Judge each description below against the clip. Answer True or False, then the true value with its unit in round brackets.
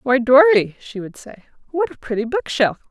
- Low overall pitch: False (260 Hz)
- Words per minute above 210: False (205 wpm)